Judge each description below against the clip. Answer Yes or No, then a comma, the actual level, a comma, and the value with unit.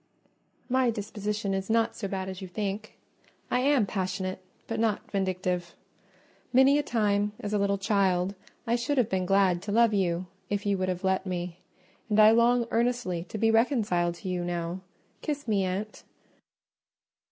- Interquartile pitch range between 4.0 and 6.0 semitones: No, average, 3.3 semitones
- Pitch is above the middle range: Yes, high, 200 Hz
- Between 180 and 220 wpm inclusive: No, average, 170 wpm